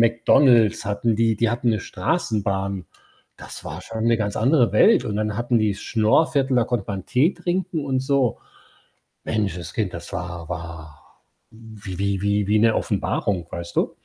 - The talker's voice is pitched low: Yes, low, 110 Hz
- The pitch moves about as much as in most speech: Yes, average, 3.4 semitones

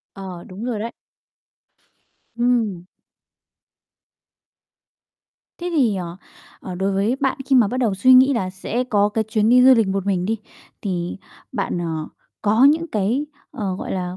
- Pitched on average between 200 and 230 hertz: Yes, high, 210 Hz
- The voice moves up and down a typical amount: Yes, average, 4.7 semitones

